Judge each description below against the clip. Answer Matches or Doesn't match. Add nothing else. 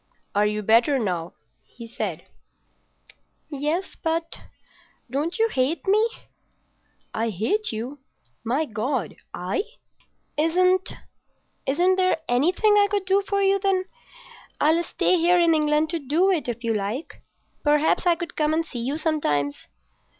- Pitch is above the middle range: Matches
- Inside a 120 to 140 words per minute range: Matches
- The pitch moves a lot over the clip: Matches